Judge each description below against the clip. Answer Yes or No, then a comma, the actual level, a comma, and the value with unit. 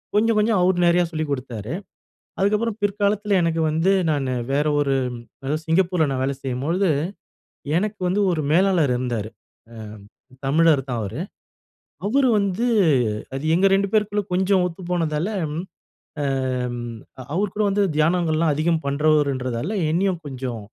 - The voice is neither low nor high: Yes, medium, 165 Hz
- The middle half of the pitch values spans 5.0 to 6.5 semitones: Yes, wide, 5.6 semitones